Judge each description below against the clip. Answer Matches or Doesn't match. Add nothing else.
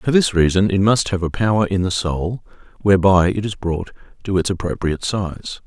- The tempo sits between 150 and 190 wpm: Doesn't match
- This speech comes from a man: Matches